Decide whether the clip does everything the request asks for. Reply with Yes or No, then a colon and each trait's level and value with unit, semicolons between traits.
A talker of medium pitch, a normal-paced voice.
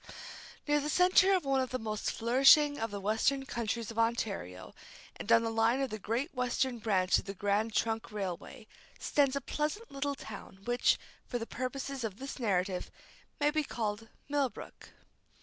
No: high, 235 Hz; average, 175 wpm